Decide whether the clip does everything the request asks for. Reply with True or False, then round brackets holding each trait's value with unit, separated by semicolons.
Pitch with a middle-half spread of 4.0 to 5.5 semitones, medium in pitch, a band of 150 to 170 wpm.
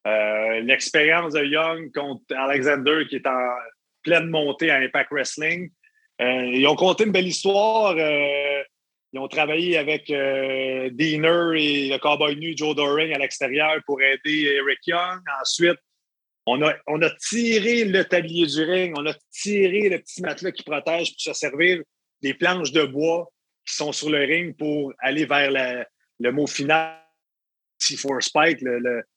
False (3.3 semitones; 150 Hz; 165 wpm)